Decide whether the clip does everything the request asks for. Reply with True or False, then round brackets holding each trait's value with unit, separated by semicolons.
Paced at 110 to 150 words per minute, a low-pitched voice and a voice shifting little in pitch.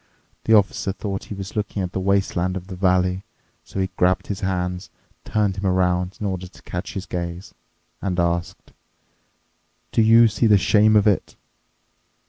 False (170 wpm; 95 Hz; 2.0 semitones)